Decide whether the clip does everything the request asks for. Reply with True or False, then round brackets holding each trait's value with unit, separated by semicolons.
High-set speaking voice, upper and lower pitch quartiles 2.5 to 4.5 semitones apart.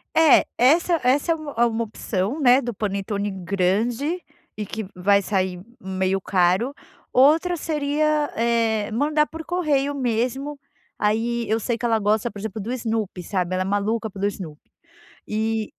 False (225 Hz; 5.6 semitones)